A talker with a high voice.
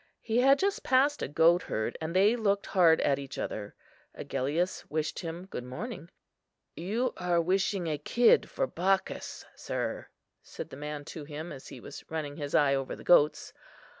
No: medium, 165 Hz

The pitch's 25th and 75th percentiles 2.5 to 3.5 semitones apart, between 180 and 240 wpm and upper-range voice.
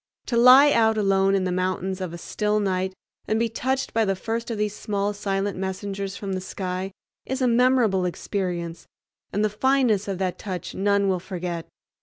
Yes: average, 2.9 semitones; average, 190 wpm; high, 200 Hz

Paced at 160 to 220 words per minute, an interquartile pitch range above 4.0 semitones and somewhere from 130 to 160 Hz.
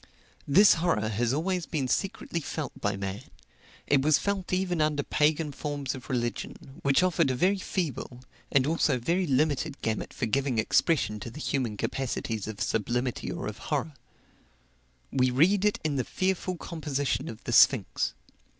Yes: average, 165 wpm; average, 5.3 semitones; medium, 140 Hz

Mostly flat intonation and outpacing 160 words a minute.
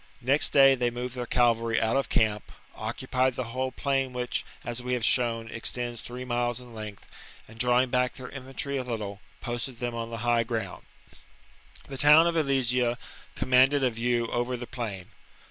Yes: narrow, 1.8 semitones; average, 180 wpm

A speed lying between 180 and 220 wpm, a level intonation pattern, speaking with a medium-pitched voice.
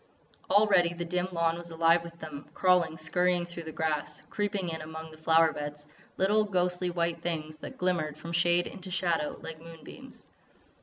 No: average, 170 wpm; narrow, 2.0 semitones; medium, 170 Hz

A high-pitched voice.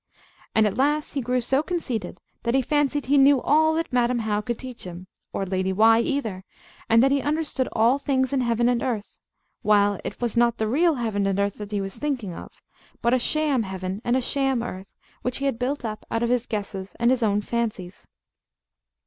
Yes: high, 235 Hz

